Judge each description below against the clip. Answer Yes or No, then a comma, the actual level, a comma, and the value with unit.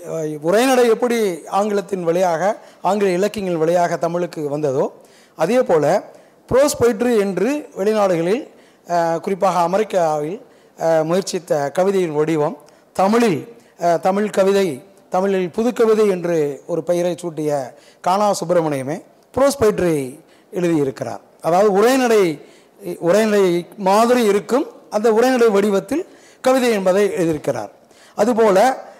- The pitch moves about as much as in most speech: Yes, average, 4.3 semitones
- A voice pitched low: No, high, 190 Hz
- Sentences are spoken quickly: No, average, 95 wpm